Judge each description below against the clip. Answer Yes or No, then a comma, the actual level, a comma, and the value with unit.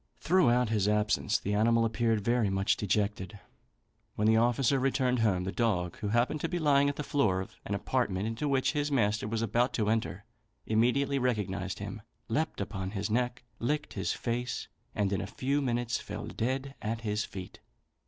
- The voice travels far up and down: No, average, 3.6 semitones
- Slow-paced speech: No, average, 185 wpm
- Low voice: Yes, low, 115 Hz